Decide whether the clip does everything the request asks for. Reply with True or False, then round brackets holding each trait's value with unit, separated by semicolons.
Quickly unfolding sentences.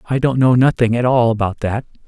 True (230 wpm)